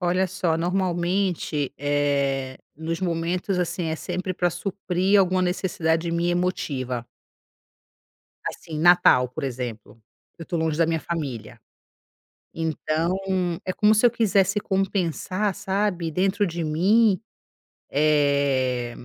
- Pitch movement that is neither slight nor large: Yes, average, 3.9 semitones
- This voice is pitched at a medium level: Yes, medium, 170 Hz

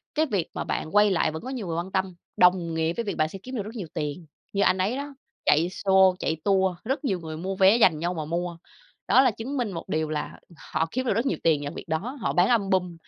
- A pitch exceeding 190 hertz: No, medium, 185 Hz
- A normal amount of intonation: Yes, average, 4.5 semitones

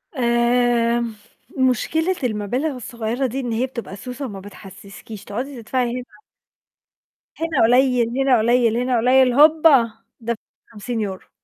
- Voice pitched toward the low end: No, high, 240 Hz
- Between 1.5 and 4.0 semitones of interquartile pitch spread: Yes, narrow, 2.5 semitones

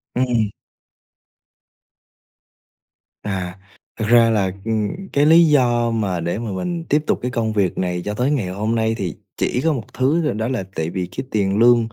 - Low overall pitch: Yes, low, 115 Hz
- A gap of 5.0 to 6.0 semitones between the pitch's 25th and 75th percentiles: No, average, 4.3 semitones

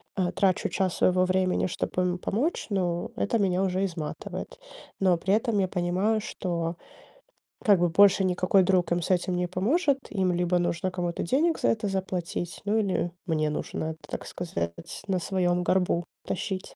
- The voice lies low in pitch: No, medium, 185 Hz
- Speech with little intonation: Yes, narrow, 1.8 semitones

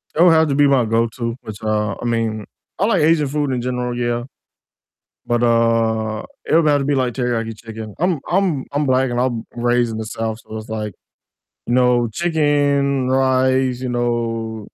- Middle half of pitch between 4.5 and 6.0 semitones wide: No, average, 3.4 semitones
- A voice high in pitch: No, low, 120 Hz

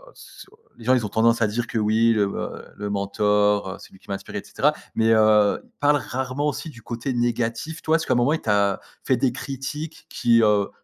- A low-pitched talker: Yes, low, 115 Hz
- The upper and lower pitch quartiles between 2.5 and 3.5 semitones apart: No, average, 4.1 semitones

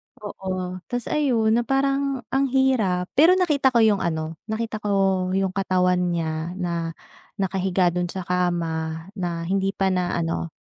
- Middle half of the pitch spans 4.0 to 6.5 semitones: Yes, average, 4.3 semitones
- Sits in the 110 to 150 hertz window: No, high, 190 Hz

